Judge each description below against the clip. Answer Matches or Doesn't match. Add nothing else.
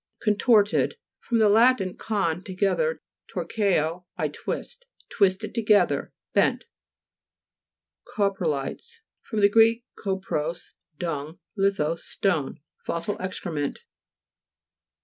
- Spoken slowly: Matches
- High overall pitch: Matches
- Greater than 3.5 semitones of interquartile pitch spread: Matches